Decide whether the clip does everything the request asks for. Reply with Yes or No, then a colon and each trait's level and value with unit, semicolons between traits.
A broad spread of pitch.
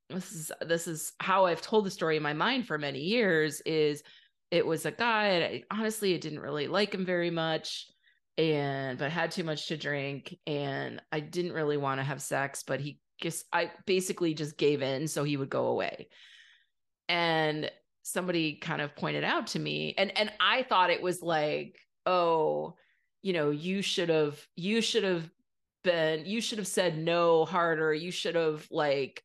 No: average, 3.6 semitones